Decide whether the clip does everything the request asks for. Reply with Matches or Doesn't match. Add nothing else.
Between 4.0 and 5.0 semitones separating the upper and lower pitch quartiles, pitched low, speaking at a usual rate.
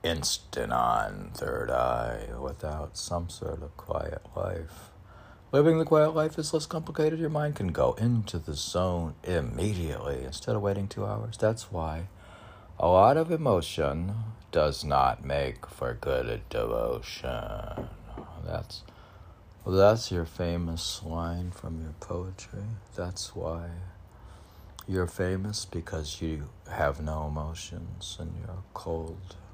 Doesn't match